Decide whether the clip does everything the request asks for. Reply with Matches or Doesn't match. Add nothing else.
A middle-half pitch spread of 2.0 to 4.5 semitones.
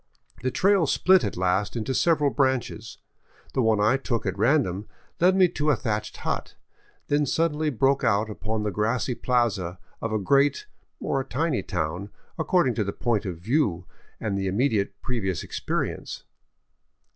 Doesn't match